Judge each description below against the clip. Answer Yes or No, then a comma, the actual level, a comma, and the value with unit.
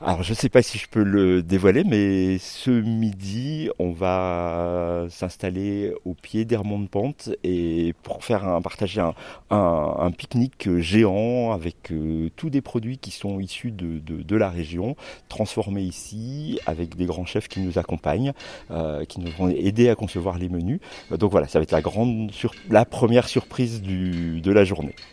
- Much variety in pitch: No, average, 4.3 semitones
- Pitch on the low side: Yes, very low, 95 Hz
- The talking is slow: No, average, 185 wpm